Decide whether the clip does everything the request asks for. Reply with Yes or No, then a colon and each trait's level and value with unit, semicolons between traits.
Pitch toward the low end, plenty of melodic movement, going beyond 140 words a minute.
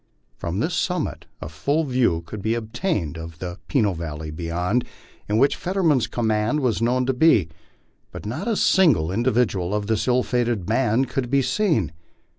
Yes: low, 115 Hz; wide, 6.4 semitones; average, 170 wpm